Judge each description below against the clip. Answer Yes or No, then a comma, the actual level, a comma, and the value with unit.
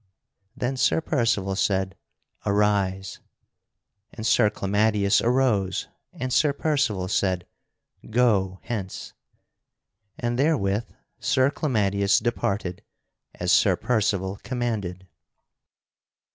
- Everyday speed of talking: No, slow, 90 wpm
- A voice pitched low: Yes, low, 105 Hz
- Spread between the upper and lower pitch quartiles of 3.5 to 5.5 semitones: Yes, average, 3.9 semitones